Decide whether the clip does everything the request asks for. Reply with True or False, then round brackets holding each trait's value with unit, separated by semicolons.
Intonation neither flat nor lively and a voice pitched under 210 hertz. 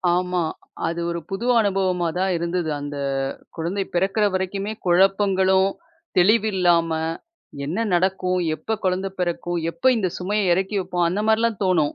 False (2.0 semitones; 185 Hz)